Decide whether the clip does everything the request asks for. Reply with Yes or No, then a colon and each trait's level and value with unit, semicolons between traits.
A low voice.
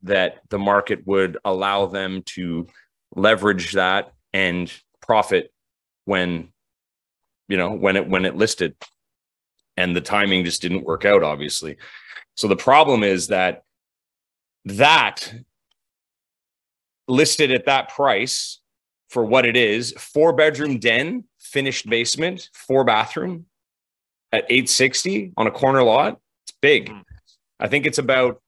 Yes: low, 100 Hz